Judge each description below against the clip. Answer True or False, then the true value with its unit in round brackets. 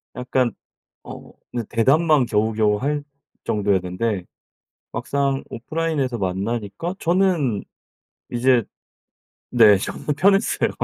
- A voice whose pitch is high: False (120 Hz)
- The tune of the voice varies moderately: False (5.8 semitones)